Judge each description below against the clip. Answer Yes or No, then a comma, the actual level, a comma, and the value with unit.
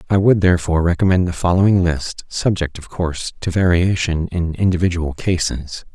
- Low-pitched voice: Yes, very low, 85 Hz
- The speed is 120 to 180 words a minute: Yes, average, 150 wpm